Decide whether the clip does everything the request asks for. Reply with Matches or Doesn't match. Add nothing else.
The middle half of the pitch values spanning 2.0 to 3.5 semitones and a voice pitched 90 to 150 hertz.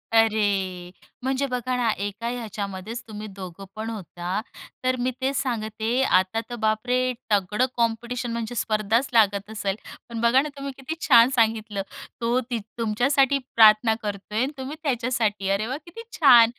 Doesn't match